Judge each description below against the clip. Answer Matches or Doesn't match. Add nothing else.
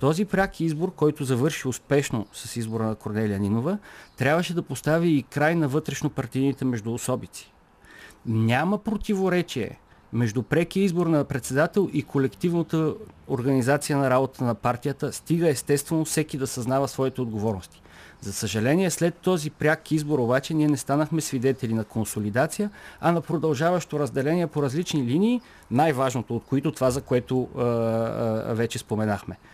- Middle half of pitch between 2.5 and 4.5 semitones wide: Doesn't match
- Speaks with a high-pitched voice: Doesn't match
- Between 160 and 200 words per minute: Doesn't match